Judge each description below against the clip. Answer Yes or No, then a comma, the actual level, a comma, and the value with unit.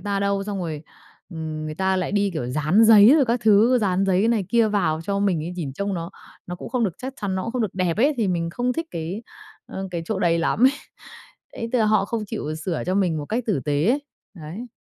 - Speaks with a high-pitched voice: Yes, high, 195 Hz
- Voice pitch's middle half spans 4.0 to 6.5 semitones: Yes, average, 4.8 semitones